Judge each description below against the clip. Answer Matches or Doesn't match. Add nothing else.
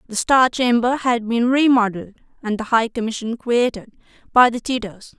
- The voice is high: Matches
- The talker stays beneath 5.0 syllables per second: Doesn't match